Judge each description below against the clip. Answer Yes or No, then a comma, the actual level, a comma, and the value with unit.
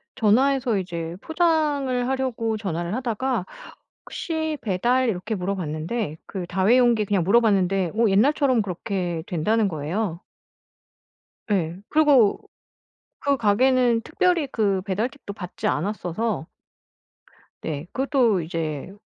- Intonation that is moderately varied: No, wide, 6.1 semitones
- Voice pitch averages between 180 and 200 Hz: No, high, 215 Hz